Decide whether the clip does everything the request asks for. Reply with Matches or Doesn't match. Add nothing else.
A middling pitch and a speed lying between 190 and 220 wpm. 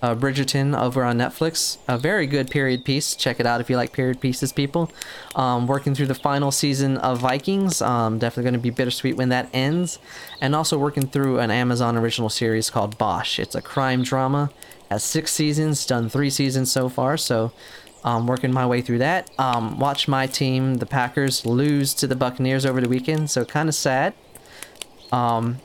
Doesn't match